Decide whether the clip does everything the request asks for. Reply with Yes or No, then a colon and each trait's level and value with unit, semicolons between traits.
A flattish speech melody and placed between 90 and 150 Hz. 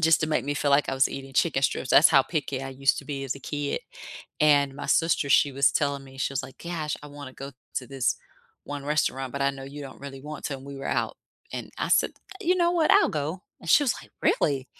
Yes: narrow, 1.9 semitones; medium, 140 Hz